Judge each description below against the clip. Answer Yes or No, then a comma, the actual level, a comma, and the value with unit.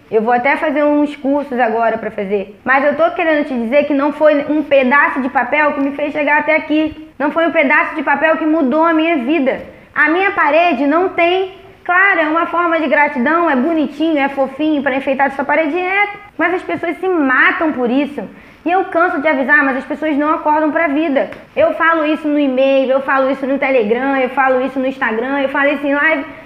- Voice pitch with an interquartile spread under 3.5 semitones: Yes, average, 2.9 semitones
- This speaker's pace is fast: Yes, fast, 225 wpm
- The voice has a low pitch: No, very high, 295 Hz